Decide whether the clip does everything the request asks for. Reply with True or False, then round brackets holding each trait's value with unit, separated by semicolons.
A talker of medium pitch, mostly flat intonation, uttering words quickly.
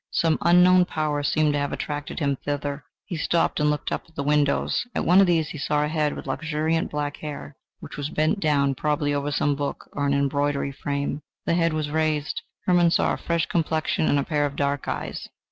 True (150 Hz; 1.8 semitones; 215 wpm)